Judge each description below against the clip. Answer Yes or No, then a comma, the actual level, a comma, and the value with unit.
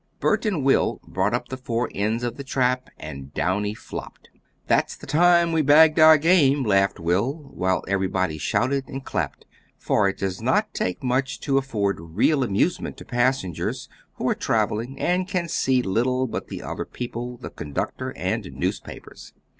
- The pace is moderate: Yes, average, 170 wpm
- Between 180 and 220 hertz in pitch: No, low, 125 Hz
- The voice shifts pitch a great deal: Yes, wide, 5.9 semitones